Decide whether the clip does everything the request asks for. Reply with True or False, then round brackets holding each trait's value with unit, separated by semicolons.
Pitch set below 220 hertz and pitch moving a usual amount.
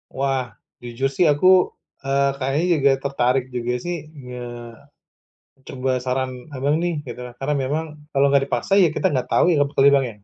False (135 Hz; 1.7 semitones)